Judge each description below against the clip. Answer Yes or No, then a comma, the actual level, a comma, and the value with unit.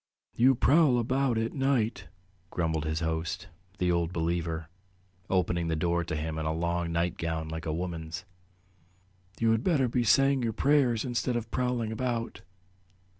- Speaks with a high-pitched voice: No, very low, 90 Hz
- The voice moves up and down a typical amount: No, wide, 6.8 semitones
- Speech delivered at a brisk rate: No, average, 155 wpm